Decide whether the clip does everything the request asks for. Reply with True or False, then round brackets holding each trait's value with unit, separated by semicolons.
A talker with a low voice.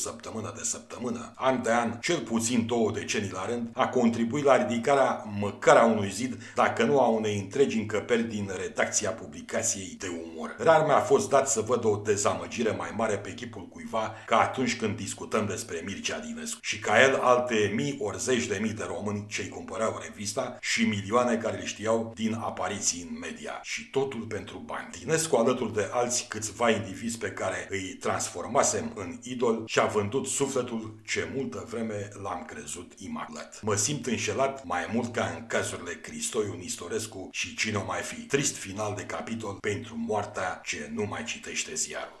True (115 Hz)